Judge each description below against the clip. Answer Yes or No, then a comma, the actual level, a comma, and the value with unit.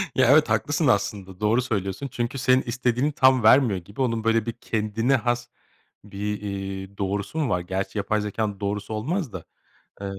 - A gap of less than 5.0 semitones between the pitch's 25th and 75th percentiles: Yes, average, 4.2 semitones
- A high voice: No, low, 110 Hz